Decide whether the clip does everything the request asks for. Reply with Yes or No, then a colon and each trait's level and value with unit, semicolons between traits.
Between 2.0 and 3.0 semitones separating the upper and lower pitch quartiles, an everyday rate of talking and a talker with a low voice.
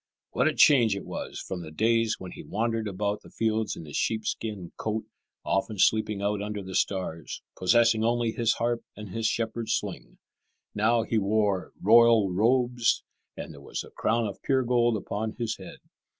Yes: narrow, 2.5 semitones; average, 180 wpm; low, 110 Hz